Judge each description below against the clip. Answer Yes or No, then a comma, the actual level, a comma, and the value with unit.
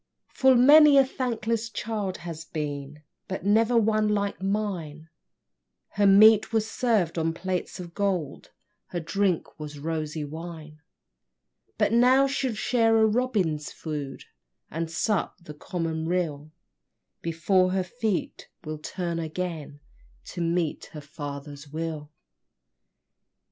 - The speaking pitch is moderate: Yes, medium, 175 Hz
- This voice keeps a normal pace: No, slow, 120 wpm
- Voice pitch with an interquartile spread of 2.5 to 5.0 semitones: No, wide, 5.6 semitones